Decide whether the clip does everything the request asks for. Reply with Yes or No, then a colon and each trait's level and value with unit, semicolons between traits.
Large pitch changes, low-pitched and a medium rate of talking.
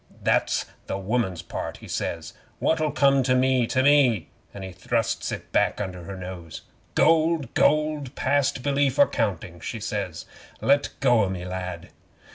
Yes: wide, 7.1 semitones; low, 120 Hz; average, 160 wpm